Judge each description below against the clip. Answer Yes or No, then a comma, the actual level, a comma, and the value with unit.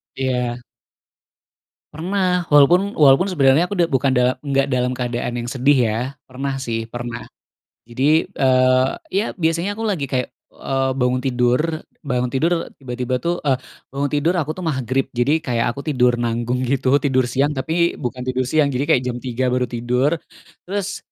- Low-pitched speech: Yes, low, 130 Hz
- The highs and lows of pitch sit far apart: No, average, 3.5 semitones